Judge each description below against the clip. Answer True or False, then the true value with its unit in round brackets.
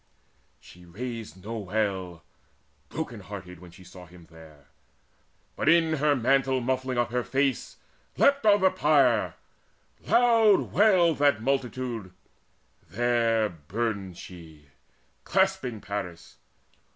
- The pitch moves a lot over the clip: True (7.3 semitones)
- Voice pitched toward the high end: False (120 Hz)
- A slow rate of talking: True (115 wpm)